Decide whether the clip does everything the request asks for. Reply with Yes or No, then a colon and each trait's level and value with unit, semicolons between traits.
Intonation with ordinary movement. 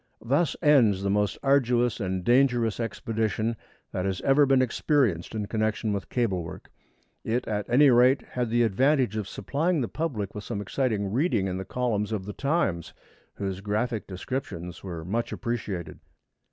Yes: average, 4.4 semitones